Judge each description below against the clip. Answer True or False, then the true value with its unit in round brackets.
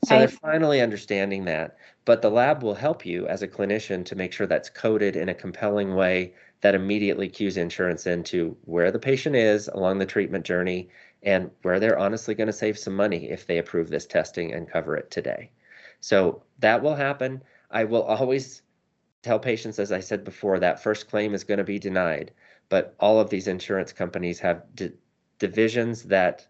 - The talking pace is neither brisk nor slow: True (190 wpm)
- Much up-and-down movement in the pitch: False (2.7 semitones)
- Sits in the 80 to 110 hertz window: True (105 Hz)